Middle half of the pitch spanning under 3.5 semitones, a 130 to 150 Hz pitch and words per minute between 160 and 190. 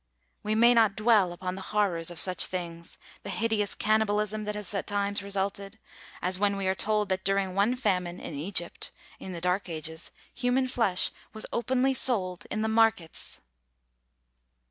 No: average, 3.0 semitones; high, 200 Hz; average, 165 wpm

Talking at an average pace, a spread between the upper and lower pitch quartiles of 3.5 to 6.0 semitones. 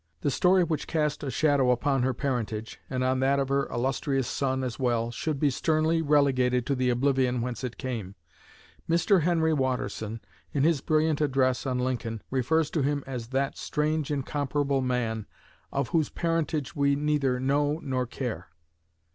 No: average, 165 wpm; average, 3.0 semitones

